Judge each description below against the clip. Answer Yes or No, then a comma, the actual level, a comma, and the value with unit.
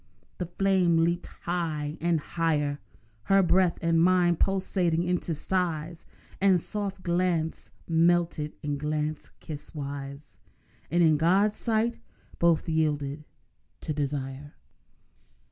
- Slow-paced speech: Yes, slow, 110 wpm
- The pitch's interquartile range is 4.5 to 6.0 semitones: No, average, 3.0 semitones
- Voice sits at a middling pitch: Yes, medium, 165 Hz